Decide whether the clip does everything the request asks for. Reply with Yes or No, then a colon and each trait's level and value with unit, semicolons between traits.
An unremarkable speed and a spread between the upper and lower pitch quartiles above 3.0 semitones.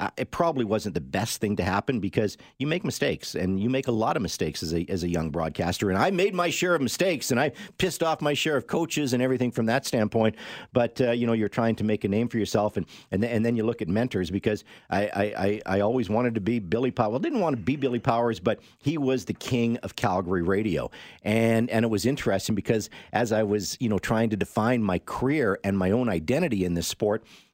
No: fast, 250 wpm; average, 3.4 semitones